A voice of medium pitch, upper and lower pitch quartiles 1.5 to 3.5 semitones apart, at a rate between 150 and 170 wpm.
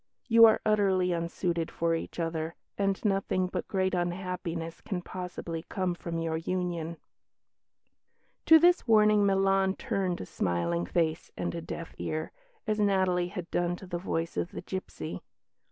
Yes: medium, 180 Hz; narrow, 2.6 semitones; average, 155 wpm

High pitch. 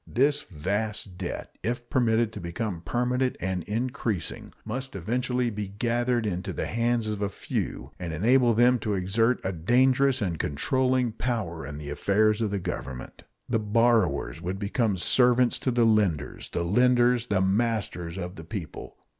No: low, 110 Hz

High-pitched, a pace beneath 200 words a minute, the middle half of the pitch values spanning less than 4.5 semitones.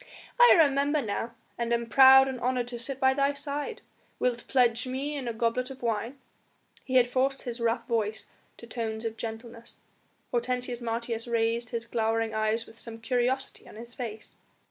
Yes: high, 240 Hz; average, 175 wpm; narrow, 2.4 semitones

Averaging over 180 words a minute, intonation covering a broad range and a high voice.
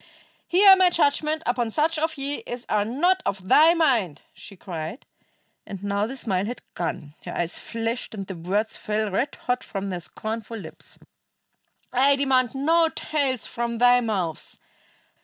No: average, 160 wpm; wide, 6.0 semitones; high, 235 Hz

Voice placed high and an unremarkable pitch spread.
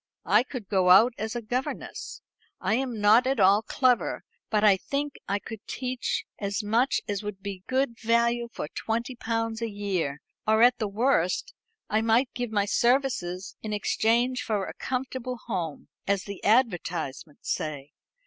Yes: high, 220 Hz; average, 3.6 semitones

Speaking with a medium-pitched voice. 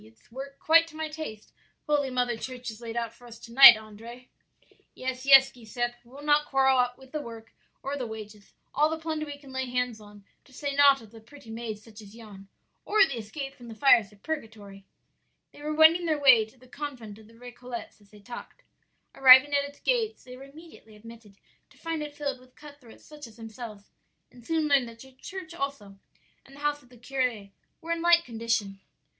No: very high, 255 Hz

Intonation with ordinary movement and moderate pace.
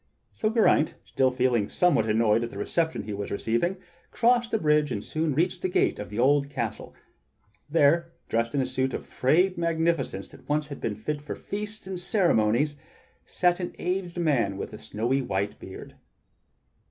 No: wide, 7.0 semitones; average, 175 wpm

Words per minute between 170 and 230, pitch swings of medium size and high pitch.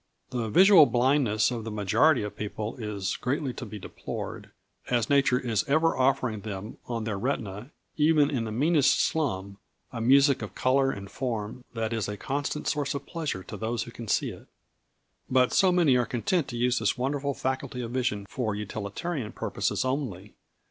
No: average, 185 wpm; average, 4.5 semitones; low, 125 Hz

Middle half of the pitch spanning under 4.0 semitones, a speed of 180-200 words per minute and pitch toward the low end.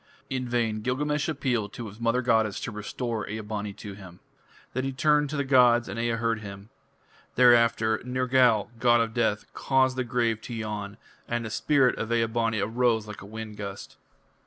Yes: average, 2.8 semitones; average, 185 wpm; low, 115 Hz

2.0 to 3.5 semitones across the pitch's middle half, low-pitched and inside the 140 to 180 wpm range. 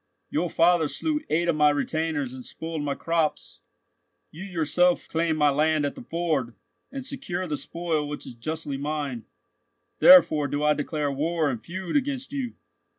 No: average, 3.1 semitones; medium, 160 Hz; average, 165 wpm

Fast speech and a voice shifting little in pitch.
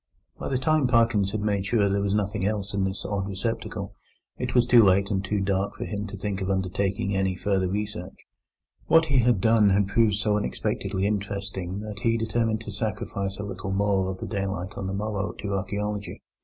Yes: fast, 210 wpm; narrow, 1.7 semitones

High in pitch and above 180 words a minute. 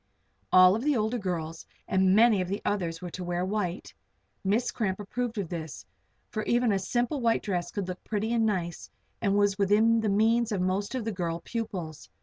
Yes: high, 200 Hz; average, 195 wpm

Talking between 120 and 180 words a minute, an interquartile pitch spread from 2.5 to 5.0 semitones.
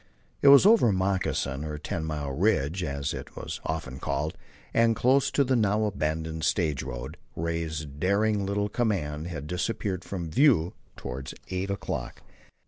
No: average, 150 wpm; wide, 5.4 semitones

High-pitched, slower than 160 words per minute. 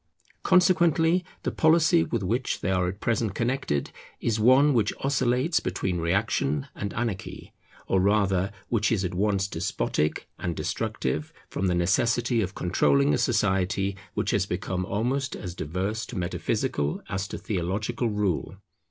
No: low, 100 Hz; average, 145 wpm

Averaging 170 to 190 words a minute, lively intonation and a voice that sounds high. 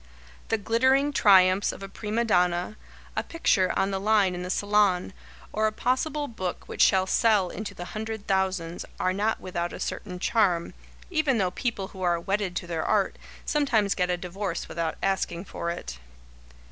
No: average, 175 wpm; average, 3.4 semitones; high, 195 Hz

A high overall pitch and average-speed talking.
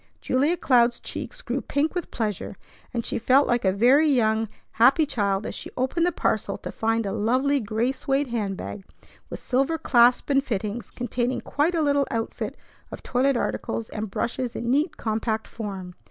Yes: high, 240 Hz; average, 180 wpm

